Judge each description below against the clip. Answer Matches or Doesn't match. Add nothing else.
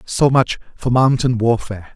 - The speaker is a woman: Doesn't match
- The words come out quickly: Doesn't match